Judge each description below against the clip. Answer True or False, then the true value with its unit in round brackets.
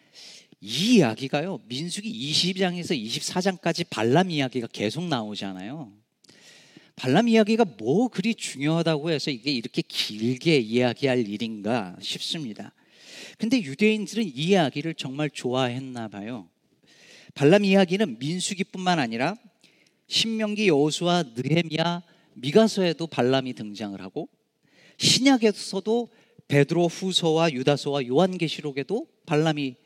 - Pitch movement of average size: False (6.4 semitones)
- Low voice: False (165 Hz)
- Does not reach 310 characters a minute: True (290 characters per minute)